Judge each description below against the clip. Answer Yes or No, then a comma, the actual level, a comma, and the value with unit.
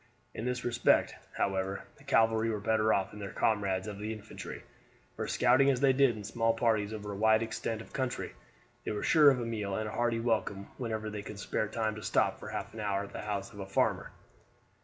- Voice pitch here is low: Yes, low, 110 Hz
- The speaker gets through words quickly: Yes, fast, 225 wpm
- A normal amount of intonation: No, narrow, 2.1 semitones